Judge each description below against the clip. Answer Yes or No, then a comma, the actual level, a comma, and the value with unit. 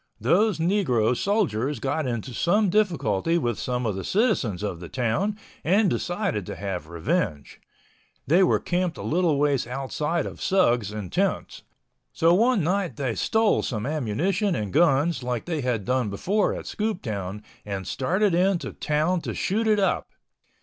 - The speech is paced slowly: No, average, 165 wpm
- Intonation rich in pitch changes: Yes, wide, 8.5 semitones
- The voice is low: No, medium, 150 Hz